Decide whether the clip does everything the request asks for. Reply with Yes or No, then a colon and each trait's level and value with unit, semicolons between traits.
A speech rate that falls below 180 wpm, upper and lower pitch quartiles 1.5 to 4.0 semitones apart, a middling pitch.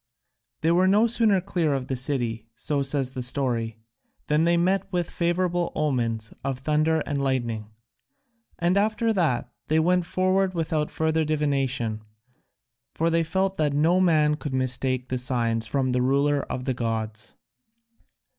No: average, 155 wpm; average, 5.2 semitones; medium, 150 Hz